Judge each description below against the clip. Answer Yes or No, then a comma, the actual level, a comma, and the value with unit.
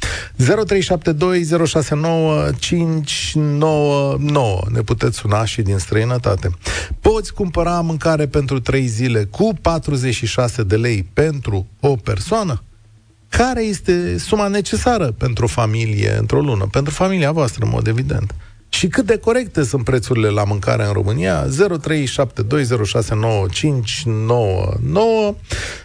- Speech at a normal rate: No, slow, 100 wpm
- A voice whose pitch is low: Yes, low, 130 Hz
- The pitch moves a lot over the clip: Yes, wide, 7.0 semitones